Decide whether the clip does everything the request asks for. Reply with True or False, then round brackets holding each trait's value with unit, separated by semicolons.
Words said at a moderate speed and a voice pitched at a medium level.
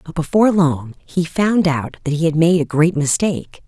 False (210 wpm; 165 Hz)